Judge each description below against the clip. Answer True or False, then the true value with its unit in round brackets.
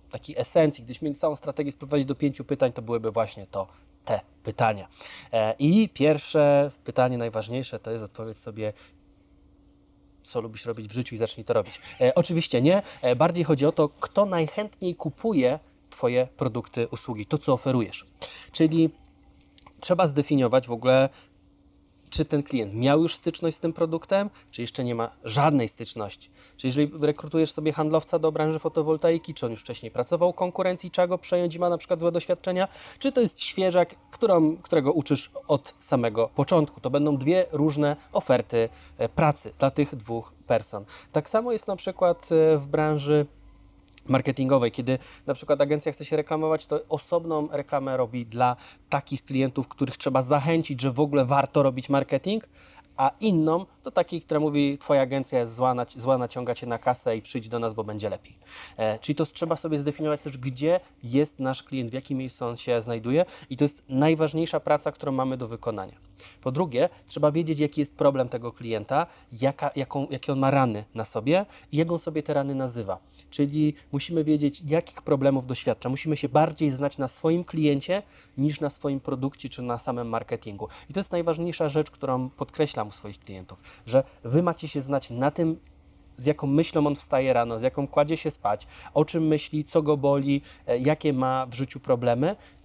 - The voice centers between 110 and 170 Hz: True (140 Hz)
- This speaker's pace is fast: True (180 wpm)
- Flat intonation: False (4.7 semitones)